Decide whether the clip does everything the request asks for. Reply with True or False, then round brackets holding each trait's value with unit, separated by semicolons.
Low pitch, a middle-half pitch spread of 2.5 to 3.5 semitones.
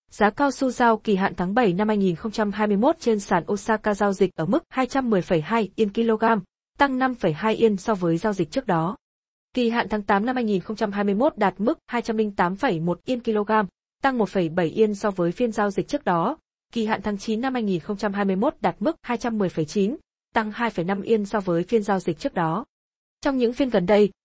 False (215 Hz; 3.2 semitones)